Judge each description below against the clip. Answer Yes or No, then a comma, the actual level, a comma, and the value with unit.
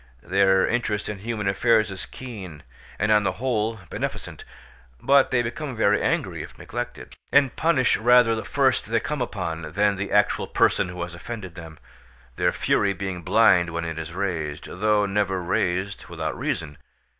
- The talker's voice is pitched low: Yes, low, 100 Hz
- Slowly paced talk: No, average, 170 wpm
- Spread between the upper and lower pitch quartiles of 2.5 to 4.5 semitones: Yes, average, 4.1 semitones